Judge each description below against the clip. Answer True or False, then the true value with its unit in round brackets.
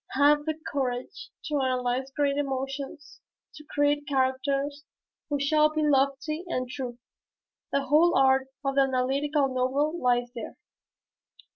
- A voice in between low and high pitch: False (275 Hz)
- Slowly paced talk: True (130 wpm)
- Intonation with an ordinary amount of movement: False (2.0 semitones)